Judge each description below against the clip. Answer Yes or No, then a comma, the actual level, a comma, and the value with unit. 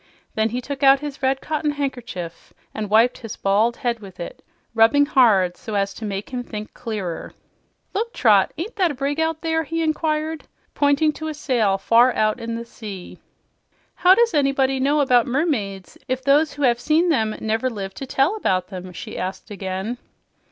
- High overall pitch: Yes, very high, 250 Hz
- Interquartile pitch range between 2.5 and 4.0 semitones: No, wide, 5.6 semitones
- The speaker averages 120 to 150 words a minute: No, average, 185 wpm